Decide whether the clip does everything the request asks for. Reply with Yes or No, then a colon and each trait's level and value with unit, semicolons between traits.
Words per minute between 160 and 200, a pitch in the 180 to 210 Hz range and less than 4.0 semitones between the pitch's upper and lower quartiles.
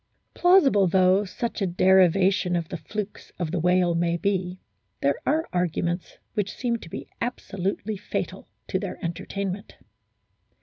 No: average, 140 wpm; medium, 185 Hz; average, 2.7 semitones